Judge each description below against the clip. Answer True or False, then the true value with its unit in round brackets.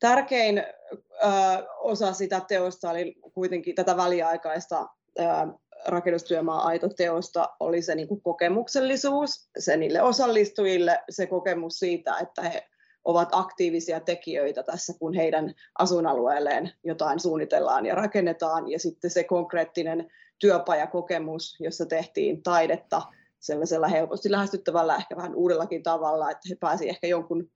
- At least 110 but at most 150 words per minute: True (120 wpm)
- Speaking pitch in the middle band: True (175 Hz)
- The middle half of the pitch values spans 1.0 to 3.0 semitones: True (2.5 semitones)